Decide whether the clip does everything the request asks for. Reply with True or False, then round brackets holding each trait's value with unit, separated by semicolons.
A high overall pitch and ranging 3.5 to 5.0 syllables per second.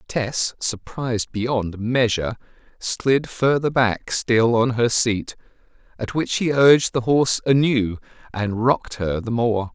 False (120 Hz; 4.0 syllables/s)